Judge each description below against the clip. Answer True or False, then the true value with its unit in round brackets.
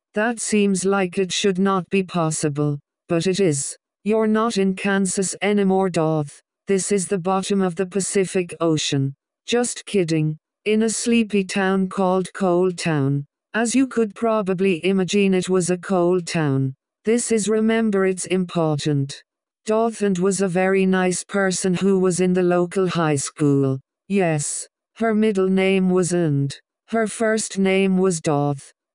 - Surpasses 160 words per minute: False (155 wpm)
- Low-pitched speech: False (190 Hz)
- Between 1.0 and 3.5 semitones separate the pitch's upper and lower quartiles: True (2.8 semitones)